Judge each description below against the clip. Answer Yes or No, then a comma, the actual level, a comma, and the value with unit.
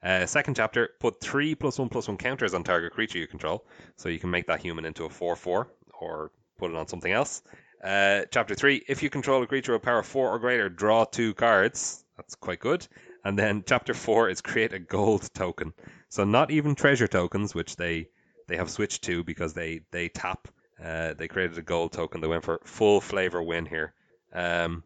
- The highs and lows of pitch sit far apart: Yes, wide, 6.7 semitones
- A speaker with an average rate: No, fast, 210 wpm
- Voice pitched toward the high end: No, very low, 95 Hz